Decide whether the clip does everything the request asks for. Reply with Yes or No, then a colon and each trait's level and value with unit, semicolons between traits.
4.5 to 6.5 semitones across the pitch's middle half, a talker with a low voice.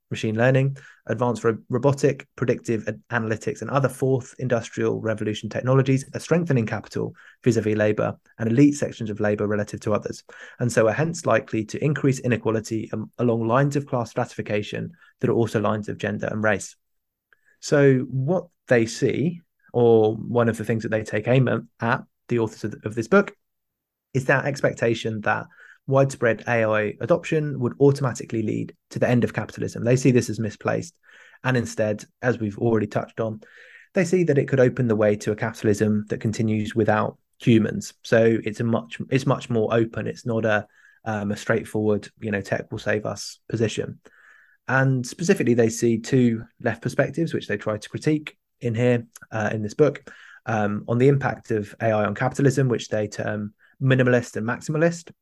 No: average, 3.4 semitones; low, 115 Hz